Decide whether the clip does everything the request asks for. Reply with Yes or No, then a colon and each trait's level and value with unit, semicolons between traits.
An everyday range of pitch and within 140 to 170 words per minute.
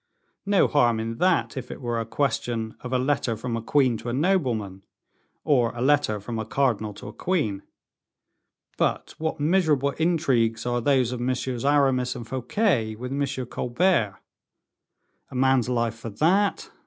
Yes: average, 3.9 semitones; average, 165 wpm